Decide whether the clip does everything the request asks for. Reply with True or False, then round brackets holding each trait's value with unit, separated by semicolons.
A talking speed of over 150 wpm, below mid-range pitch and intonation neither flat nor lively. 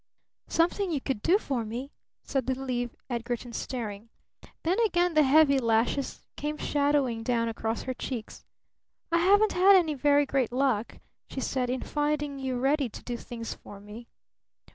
False (165 wpm; 265 Hz; 4.0 semitones)